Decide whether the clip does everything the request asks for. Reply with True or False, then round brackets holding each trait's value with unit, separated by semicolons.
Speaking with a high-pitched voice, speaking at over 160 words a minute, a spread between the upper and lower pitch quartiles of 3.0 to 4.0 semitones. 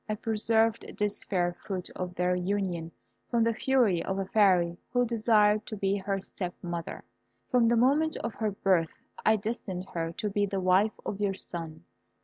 True (200 Hz; 180 wpm; 3.4 semitones)